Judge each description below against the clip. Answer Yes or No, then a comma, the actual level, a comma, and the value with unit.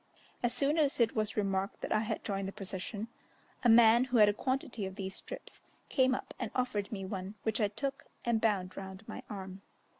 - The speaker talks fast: Yes, fast, 210 wpm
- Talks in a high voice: Yes, high, 215 Hz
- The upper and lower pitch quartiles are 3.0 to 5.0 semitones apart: Yes, average, 3.6 semitones